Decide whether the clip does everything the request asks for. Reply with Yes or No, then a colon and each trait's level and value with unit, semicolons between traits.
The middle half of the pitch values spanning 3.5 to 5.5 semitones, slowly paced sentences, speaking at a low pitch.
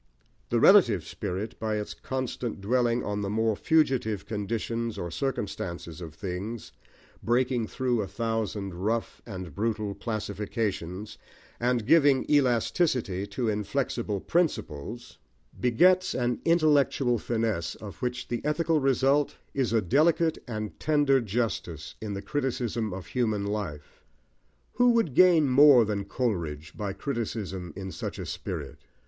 Yes: average, 4.6 semitones; slow, 130 wpm; low, 115 Hz